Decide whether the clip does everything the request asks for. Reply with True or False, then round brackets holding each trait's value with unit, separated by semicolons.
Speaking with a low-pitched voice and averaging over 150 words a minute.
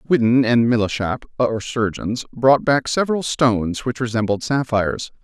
False (120 Hz; 135 wpm)